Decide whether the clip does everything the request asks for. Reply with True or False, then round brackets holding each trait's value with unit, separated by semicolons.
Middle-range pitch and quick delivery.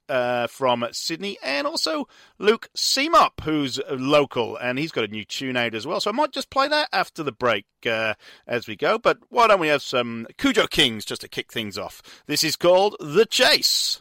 True (155 Hz; 210 wpm)